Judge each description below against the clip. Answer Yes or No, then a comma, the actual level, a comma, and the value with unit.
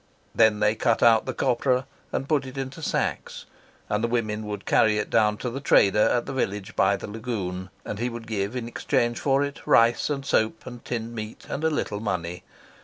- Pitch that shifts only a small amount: No, average, 3.2 semitones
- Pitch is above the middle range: No, low, 115 Hz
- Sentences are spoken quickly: Yes, fast, 210 wpm